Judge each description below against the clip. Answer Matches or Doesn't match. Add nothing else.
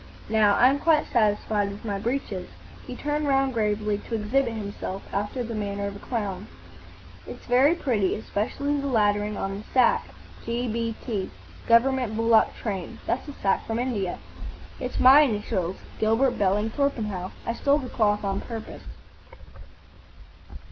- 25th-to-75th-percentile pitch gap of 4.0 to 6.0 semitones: Doesn't match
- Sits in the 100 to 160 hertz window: Doesn't match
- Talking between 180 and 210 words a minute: Doesn't match